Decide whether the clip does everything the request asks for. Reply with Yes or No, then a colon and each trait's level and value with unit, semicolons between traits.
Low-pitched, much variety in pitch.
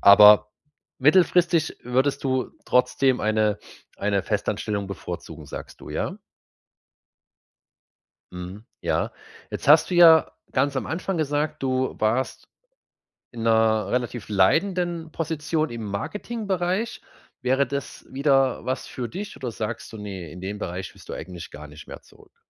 Yes: low, 125 Hz; wide, 6.9 semitones